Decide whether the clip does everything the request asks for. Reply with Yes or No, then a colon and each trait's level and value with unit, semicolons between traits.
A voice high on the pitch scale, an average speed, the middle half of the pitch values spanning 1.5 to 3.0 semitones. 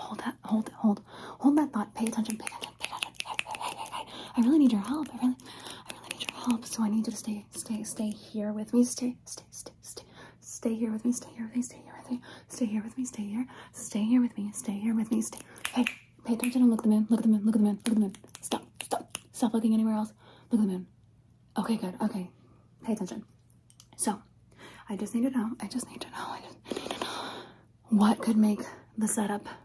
No: high, 225 Hz; fast, 265 wpm; narrow, 2.4 semitones